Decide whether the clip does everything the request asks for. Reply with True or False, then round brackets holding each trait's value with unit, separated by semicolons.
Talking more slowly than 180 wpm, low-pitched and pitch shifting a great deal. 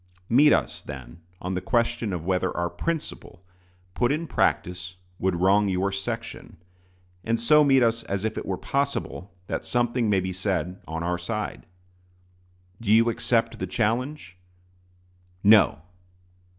False (145 wpm; 100 Hz; 4.5 semitones)